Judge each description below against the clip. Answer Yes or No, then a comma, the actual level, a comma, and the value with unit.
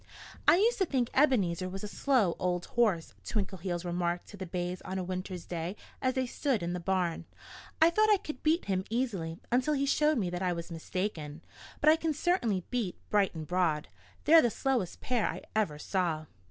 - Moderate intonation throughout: No, wide, 6.8 semitones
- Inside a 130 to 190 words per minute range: No, average, 200 wpm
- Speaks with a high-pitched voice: Yes, high, 195 Hz